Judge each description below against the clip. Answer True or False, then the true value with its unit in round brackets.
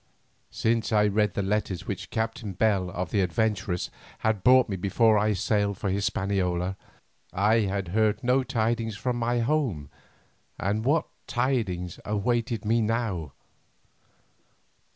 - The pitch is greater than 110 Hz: False (105 Hz)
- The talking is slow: True (130 wpm)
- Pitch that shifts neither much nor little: True (3.2 semitones)